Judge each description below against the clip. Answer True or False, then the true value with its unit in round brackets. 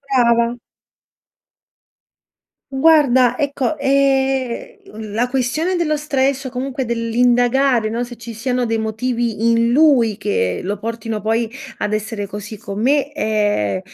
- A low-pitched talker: False (240 Hz)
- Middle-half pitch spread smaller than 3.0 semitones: False (3.3 semitones)